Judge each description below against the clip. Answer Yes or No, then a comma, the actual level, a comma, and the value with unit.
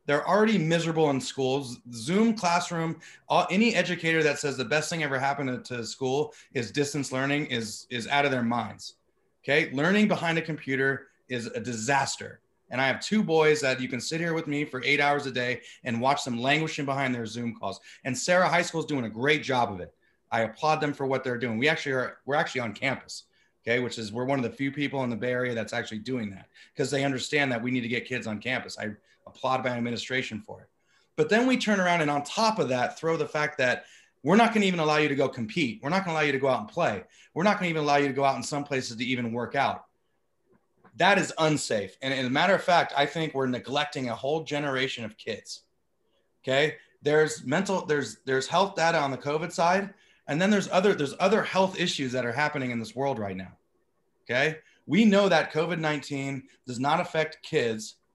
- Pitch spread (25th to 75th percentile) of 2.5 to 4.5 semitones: Yes, average, 4.1 semitones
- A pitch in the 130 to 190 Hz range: Yes, medium, 140 Hz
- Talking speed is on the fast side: Yes, fast, 230 wpm